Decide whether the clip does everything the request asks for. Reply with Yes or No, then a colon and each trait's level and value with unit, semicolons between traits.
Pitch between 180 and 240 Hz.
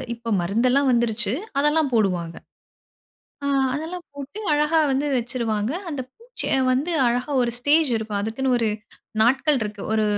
No: very high, 255 Hz